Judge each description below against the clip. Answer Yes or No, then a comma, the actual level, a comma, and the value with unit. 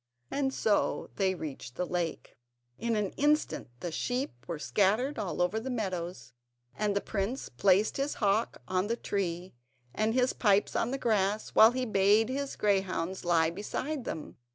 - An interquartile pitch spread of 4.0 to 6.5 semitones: Yes, average, 4.6 semitones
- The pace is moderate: Yes, average, 165 wpm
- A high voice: Yes, high, 205 Hz